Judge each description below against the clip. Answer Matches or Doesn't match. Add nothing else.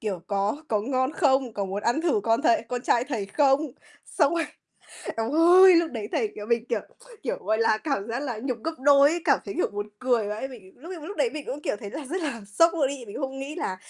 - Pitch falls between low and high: Doesn't match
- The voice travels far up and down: Matches